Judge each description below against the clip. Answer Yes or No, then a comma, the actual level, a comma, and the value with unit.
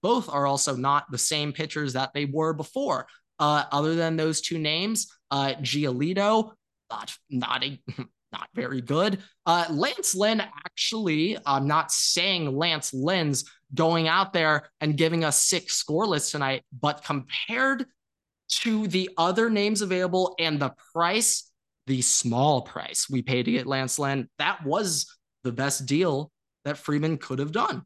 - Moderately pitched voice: Yes, medium, 155 Hz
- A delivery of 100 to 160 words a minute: Yes, average, 155 wpm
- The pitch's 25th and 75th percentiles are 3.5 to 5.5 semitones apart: Yes, average, 4.9 semitones